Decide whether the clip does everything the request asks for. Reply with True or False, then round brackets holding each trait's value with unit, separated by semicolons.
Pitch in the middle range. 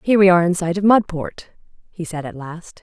True (175 Hz)